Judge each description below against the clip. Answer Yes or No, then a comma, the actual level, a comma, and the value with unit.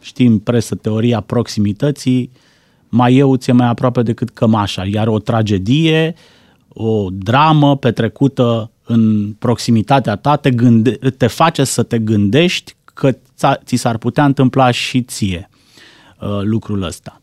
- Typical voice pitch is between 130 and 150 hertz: No, low, 120 Hz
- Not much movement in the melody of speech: No, average, 3.2 semitones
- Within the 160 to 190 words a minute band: No, average, 130 wpm